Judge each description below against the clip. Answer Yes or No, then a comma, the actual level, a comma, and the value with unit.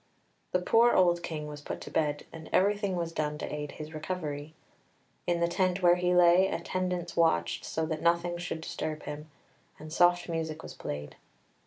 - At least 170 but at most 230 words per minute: Yes, average, 180 wpm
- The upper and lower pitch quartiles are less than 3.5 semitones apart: Yes, narrow, 2.5 semitones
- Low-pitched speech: No, medium, 170 Hz